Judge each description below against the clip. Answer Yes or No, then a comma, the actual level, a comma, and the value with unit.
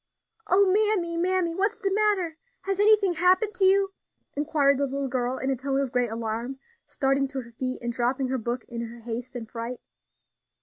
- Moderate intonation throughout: No, wide, 7.3 semitones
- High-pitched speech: Yes, very high, 275 Hz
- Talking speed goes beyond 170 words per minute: Yes, average, 190 wpm